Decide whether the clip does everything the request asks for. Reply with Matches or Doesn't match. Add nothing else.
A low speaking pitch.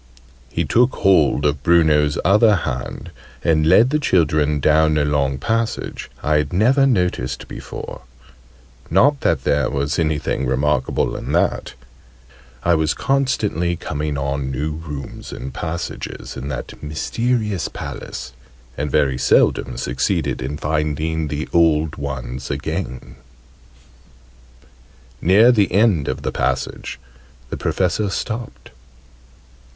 Matches